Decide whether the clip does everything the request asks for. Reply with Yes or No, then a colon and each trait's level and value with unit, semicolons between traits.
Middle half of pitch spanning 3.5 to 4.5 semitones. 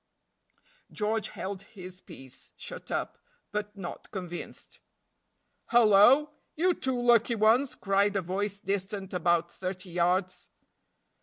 No: average, 3.0 semitones